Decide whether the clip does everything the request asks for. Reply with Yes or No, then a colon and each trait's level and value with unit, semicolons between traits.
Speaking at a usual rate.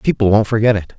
No: fast, 245 wpm